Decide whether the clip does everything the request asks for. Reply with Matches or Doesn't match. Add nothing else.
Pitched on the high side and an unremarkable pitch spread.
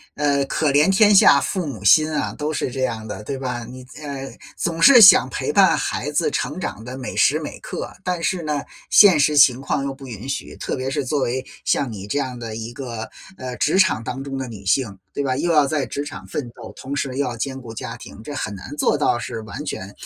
Doesn't match